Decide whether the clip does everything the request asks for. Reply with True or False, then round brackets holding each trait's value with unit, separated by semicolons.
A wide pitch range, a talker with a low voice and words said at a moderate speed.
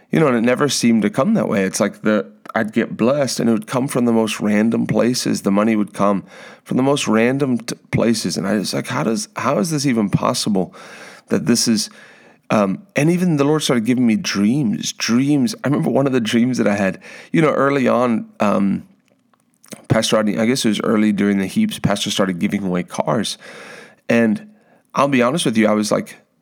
False (7.3 semitones; 120 Hz; 220 wpm)